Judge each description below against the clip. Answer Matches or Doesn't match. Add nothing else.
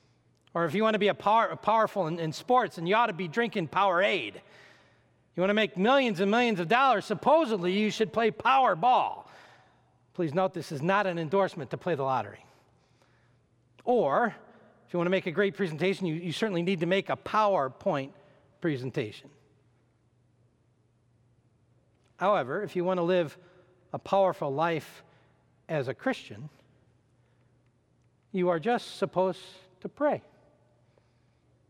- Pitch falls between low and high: Matches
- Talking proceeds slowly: Doesn't match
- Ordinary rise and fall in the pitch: Doesn't match